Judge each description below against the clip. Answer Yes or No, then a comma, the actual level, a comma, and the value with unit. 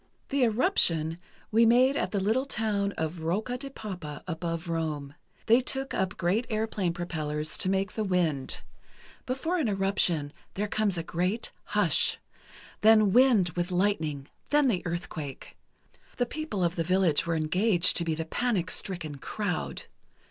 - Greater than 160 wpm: No, average, 150 wpm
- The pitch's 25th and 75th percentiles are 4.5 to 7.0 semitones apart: Yes, average, 5.1 semitones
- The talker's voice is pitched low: No, medium, 185 Hz